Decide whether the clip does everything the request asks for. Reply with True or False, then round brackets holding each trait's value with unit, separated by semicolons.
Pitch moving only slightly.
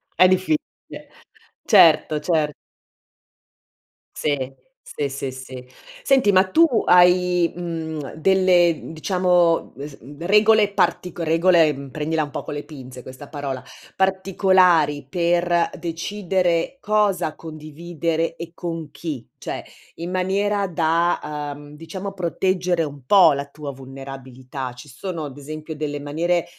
False (3.8 semitones)